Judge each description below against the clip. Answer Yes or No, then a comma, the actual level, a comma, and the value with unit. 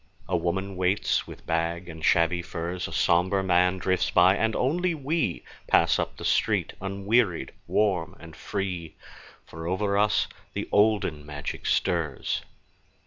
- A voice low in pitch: Yes, very low, 90 Hz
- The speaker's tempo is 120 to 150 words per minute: Yes, average, 140 wpm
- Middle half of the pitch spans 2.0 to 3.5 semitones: Yes, average, 3.1 semitones